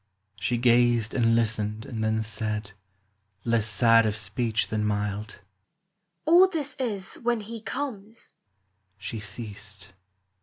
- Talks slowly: Yes, slow, 130 wpm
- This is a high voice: No, low, 115 Hz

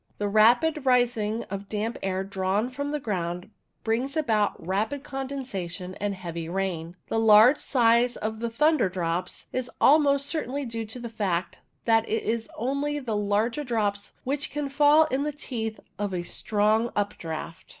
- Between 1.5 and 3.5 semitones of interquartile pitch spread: No, average, 5.2 semitones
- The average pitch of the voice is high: Yes, high, 225 Hz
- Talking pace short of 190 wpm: Yes, average, 160 wpm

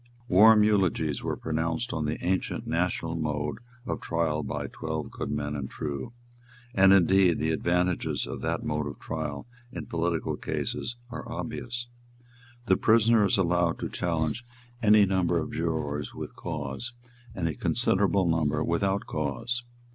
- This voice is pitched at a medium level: No, very low, 85 Hz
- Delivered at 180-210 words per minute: No, average, 145 wpm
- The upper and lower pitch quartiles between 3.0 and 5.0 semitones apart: Yes, average, 4.1 semitones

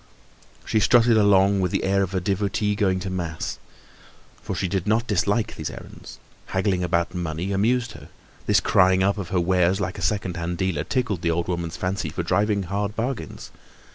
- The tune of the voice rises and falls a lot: No, narrow, 2.6 semitones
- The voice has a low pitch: Yes, very low, 95 Hz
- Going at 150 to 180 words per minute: No, average, 190 wpm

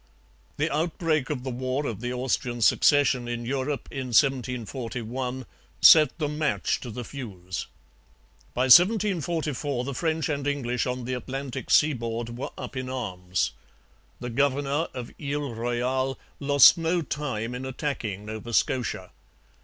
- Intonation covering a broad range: No, average, 3.1 semitones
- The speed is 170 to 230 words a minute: No, average, 140 wpm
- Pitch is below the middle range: Yes, low, 130 Hz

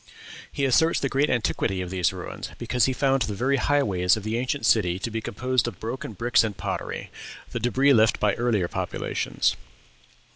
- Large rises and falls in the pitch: No, average, 4.6 semitones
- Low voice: Yes, low, 115 Hz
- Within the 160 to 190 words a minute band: Yes, average, 185 wpm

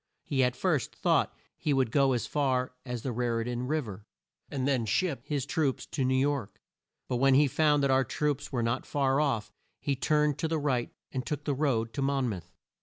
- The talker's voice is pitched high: No, low, 135 Hz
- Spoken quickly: Yes, fast, 220 wpm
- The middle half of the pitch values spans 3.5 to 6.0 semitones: No, average, 2.9 semitones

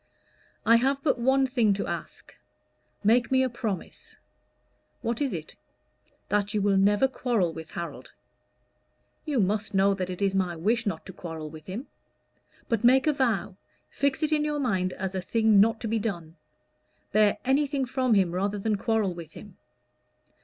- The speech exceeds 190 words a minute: No, average, 175 wpm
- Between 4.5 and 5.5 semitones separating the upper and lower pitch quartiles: Yes, average, 4.9 semitones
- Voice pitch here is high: Yes, high, 215 Hz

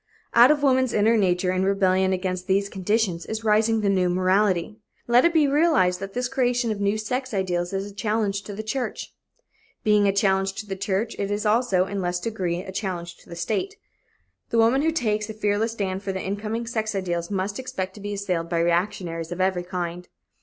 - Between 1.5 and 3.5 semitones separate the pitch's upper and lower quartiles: Yes, average, 3.1 semitones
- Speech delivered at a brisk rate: Yes, fast, 210 wpm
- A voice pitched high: Yes, high, 200 Hz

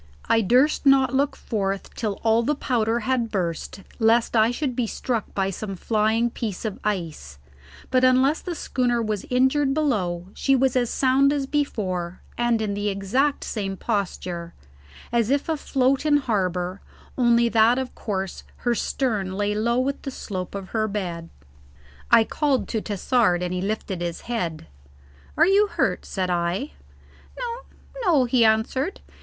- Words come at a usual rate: Yes, average, 160 wpm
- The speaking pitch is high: Yes, high, 230 Hz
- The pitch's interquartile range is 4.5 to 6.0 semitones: Yes, average, 5.1 semitones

